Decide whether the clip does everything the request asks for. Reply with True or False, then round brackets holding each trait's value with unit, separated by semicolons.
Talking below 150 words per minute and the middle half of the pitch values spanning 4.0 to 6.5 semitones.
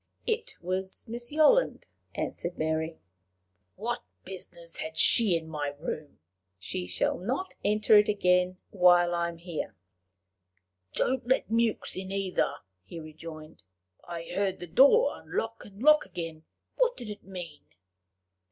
True (135 wpm; 5.3 semitones)